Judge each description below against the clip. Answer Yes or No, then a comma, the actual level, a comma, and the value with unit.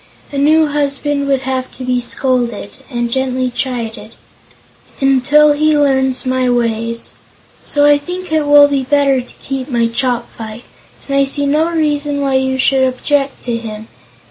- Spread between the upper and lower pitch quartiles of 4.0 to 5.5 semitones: No, average, 2.7 semitones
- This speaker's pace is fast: No, average, 160 wpm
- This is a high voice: Yes, very high, 265 Hz